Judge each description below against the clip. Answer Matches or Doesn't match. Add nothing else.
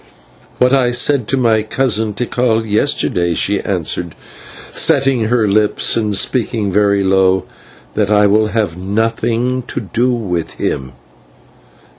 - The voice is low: Matches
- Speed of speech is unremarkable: Doesn't match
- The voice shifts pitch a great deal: Doesn't match